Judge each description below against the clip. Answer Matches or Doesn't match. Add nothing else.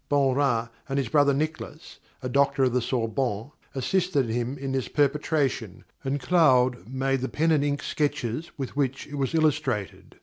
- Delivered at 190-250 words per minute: Doesn't match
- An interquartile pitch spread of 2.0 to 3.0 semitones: Matches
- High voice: Doesn't match